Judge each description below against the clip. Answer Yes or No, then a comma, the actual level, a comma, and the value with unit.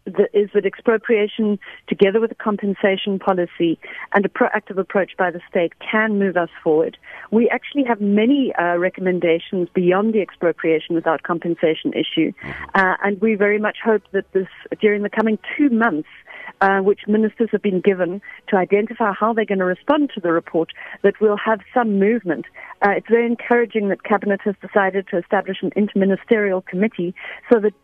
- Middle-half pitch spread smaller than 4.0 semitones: Yes, average, 2.8 semitones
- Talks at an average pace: Yes, average, 170 wpm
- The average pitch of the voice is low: No, high, 200 Hz